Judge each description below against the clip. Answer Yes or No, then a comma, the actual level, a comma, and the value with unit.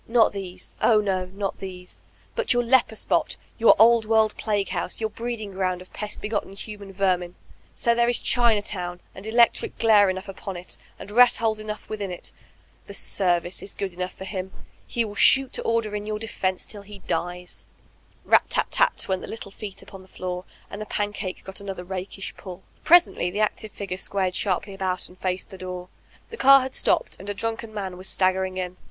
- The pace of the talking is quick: Yes, fast, 210 wpm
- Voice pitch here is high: Yes, high, 200 Hz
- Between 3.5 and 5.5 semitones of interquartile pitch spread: No, average, 2.8 semitones